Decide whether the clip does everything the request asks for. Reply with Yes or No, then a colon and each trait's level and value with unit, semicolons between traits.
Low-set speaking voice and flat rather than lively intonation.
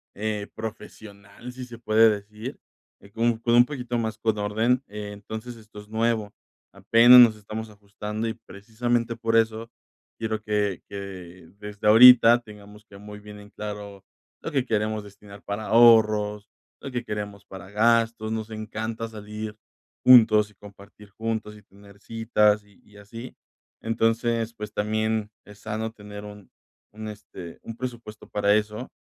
Yes: low, 110 Hz; narrow, 1.7 semitones